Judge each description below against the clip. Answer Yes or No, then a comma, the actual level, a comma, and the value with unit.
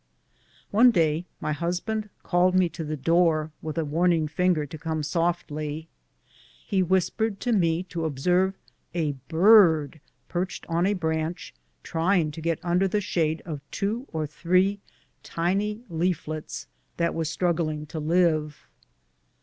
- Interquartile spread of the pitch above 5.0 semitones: No, average, 2.8 semitones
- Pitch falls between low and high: Yes, medium, 170 Hz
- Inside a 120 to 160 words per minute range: Yes, average, 140 wpm